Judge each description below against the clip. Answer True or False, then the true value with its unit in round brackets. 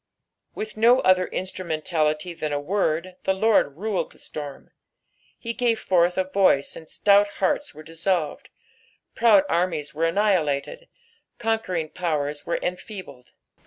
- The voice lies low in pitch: False (180 Hz)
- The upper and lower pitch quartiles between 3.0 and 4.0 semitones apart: False (4.7 semitones)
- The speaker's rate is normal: False (130 wpm)